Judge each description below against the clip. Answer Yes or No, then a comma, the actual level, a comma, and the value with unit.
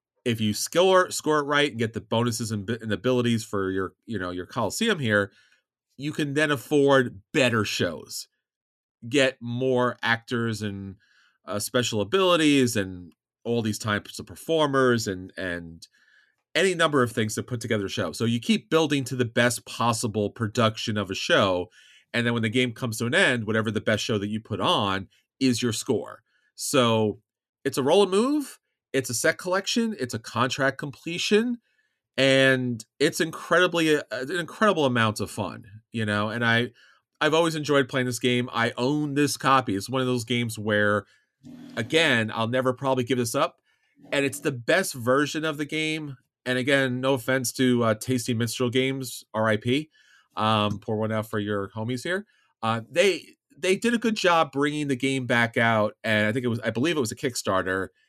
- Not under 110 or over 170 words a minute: No, average, 185 wpm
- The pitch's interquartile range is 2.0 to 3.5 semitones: No, average, 4.3 semitones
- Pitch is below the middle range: Yes, low, 125 Hz